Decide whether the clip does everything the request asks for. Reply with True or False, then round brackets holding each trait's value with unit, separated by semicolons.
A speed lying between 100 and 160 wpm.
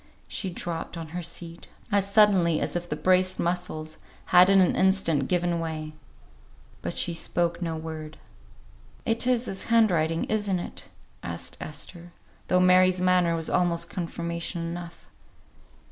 True (145 wpm)